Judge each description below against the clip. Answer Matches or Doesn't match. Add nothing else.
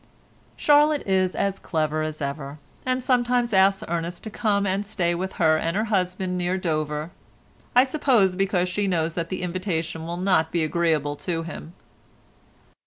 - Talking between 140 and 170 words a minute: Matches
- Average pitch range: Matches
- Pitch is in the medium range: Matches